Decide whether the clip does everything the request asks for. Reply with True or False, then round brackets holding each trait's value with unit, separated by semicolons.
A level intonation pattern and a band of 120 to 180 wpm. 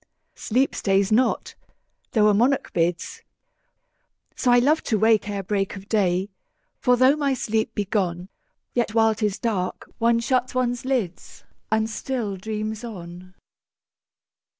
False (3.8 semitones; 145 wpm)